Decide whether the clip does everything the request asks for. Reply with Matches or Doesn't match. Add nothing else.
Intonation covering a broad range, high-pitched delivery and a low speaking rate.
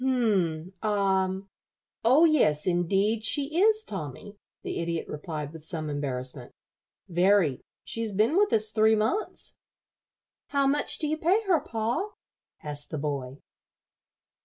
Matches